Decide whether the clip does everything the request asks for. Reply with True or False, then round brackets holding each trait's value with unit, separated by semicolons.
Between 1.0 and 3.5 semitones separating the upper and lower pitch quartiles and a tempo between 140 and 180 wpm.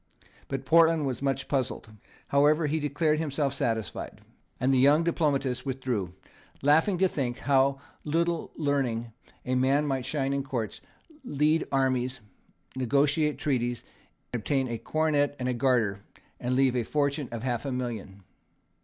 True (2.8 semitones; 145 wpm)